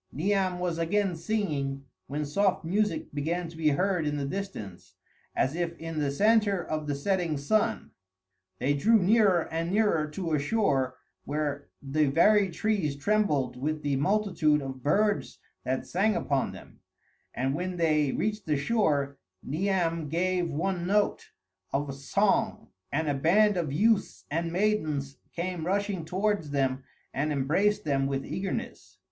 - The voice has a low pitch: No, medium, 165 Hz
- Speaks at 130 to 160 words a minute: Yes, average, 150 wpm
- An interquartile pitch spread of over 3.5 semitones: Yes, wide, 5.4 semitones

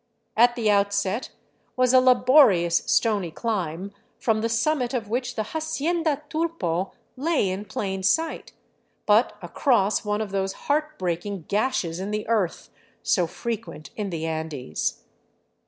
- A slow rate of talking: No, average, 145 wpm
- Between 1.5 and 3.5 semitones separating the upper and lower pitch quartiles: No, average, 5.1 semitones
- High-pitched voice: Yes, high, 210 Hz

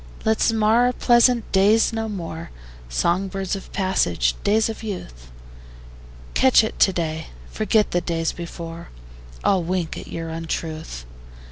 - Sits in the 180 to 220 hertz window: Yes, medium, 185 Hz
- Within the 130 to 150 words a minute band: Yes, average, 140 wpm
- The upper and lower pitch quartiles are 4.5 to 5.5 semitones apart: Yes, average, 5.0 semitones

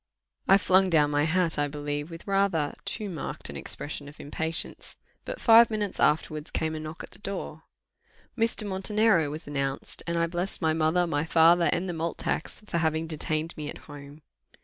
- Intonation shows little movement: No, average, 3.7 semitones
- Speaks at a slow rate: No, average, 190 wpm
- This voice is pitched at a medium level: Yes, medium, 160 Hz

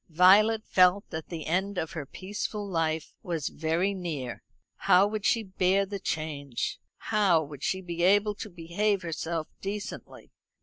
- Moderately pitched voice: Yes, medium, 180 Hz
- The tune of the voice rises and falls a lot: No, average, 3.8 semitones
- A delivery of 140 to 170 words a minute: Yes, average, 155 wpm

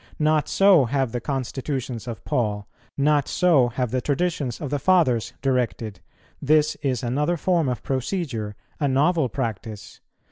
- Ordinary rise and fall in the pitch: Yes, average, 4.1 semitones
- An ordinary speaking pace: Yes, average, 145 wpm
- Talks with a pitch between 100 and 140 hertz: Yes, low, 135 Hz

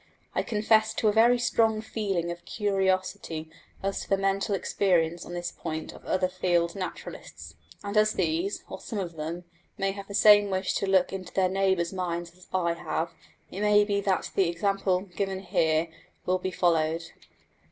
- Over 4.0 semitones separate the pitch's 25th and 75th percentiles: No, average, 2.8 semitones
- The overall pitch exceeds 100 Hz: Yes, high, 190 Hz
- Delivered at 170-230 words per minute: Yes, average, 180 wpm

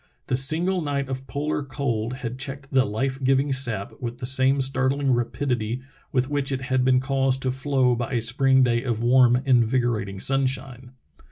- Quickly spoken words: No, average, 175 wpm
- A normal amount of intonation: No, narrow, 1.9 semitones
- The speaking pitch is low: Yes, low, 130 Hz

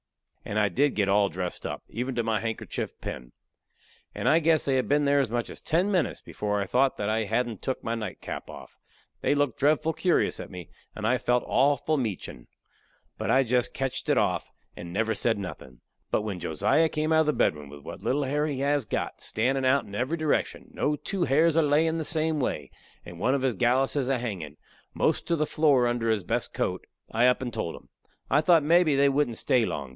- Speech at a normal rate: No, fast, 220 wpm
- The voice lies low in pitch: Yes, low, 130 Hz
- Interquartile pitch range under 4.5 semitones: No, average, 5.3 semitones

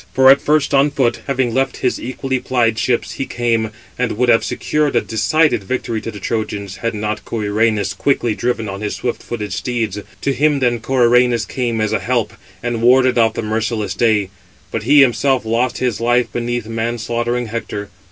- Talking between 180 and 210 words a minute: Yes, average, 190 wpm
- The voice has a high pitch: No, low, 120 Hz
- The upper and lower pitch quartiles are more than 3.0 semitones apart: No, narrow, 2.5 semitones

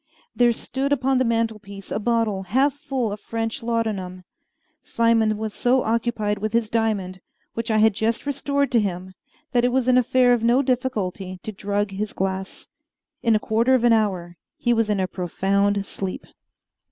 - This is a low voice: No, high, 225 Hz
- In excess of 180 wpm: No, average, 175 wpm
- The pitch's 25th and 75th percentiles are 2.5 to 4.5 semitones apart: Yes, average, 3.2 semitones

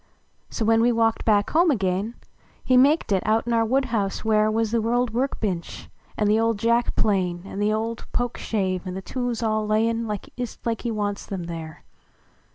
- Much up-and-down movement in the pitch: No, narrow, 2.4 semitones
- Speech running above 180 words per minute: Yes, average, 190 wpm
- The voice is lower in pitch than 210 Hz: No, high, 220 Hz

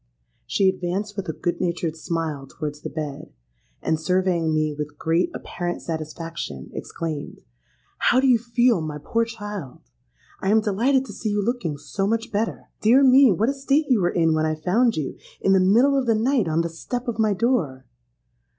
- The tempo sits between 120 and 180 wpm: No, average, 190 wpm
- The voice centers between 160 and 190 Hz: Yes, medium, 185 Hz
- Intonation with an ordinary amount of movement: No, wide, 6.4 semitones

